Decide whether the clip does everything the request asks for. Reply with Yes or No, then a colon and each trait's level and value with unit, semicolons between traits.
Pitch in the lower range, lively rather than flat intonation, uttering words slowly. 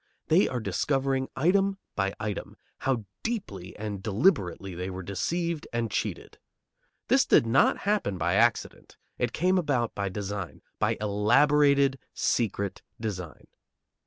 Yes: low, 115 Hz; wide, 6.8 semitones; slow, 130 wpm